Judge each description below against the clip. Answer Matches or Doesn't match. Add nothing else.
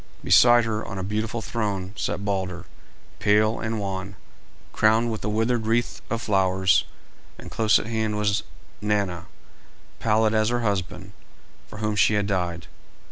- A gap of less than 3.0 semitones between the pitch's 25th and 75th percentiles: Matches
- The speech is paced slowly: Doesn't match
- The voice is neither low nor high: Doesn't match